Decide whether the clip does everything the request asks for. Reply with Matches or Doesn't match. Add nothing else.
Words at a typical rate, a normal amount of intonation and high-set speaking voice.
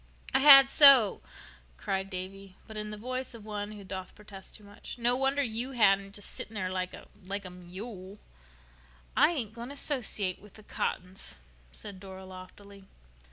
Matches